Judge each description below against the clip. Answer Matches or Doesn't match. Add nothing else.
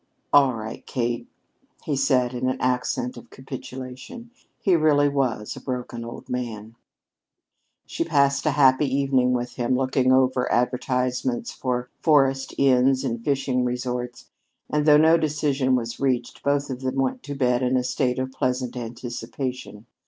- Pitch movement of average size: Doesn't match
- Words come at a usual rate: Matches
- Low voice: Matches